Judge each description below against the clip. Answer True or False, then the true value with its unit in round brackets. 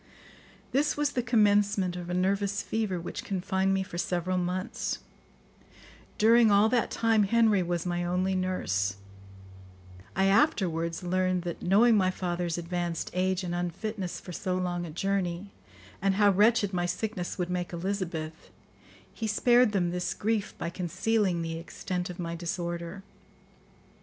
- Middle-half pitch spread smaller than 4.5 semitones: True (2.7 semitones)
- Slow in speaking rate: False (145 wpm)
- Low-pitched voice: False (185 Hz)